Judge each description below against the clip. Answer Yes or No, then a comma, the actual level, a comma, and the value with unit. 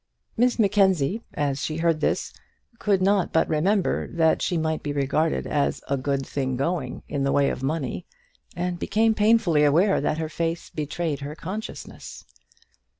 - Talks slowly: No, average, 160 wpm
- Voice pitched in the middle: Yes, medium, 160 Hz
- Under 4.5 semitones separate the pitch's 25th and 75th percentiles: No, average, 4.8 semitones